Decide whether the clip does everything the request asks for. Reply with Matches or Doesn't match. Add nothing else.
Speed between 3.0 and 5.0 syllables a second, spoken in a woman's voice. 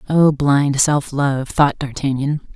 Matches